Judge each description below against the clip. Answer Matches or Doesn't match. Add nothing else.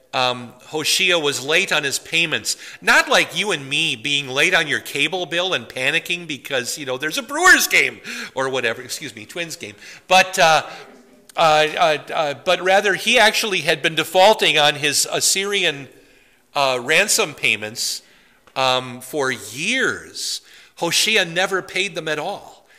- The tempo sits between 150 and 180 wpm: Matches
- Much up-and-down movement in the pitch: Matches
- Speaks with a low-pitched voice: Doesn't match